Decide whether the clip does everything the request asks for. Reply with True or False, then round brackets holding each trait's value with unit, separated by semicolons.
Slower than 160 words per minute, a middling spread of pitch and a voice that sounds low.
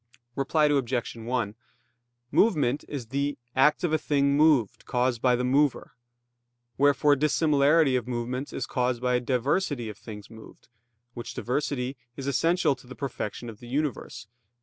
True (150 wpm; 3.0 semitones; 130 Hz)